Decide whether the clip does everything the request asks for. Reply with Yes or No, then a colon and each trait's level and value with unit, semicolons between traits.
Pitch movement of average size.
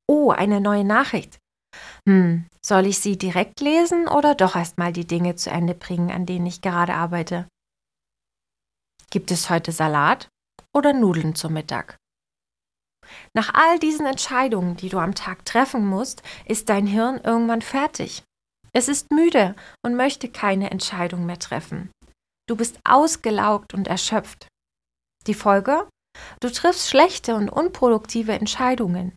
No: wide, 6.1 semitones